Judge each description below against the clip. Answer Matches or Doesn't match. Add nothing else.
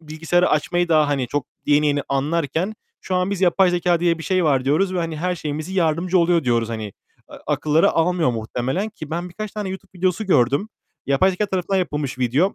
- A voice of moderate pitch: Matches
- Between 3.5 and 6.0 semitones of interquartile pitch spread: Matches